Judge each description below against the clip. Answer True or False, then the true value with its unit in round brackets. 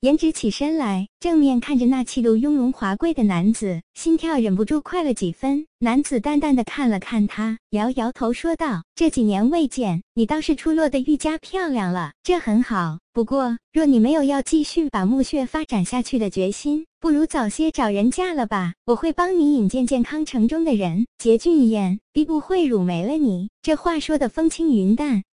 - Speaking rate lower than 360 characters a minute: True (280 characters per minute)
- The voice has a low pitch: False (255 Hz)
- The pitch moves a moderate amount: False (5.8 semitones)